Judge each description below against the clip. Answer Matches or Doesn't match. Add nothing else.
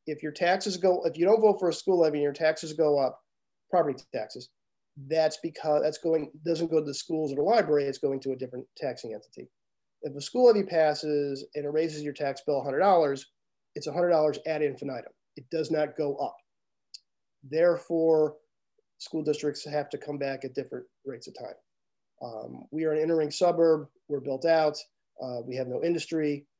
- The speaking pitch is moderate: Matches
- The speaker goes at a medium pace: Matches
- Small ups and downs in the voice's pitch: Matches